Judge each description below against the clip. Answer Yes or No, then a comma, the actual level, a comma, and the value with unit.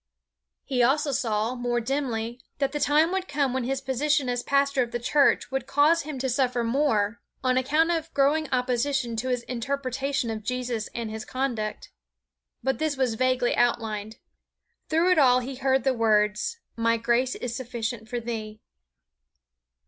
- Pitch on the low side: No, very high, 255 Hz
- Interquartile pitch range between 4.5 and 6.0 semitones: No, average, 3.0 semitones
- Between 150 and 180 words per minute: Yes, average, 165 wpm